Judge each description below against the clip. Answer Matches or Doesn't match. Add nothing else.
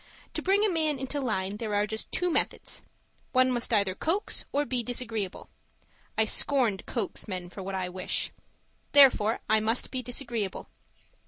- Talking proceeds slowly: Doesn't match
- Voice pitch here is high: Matches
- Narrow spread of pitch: Doesn't match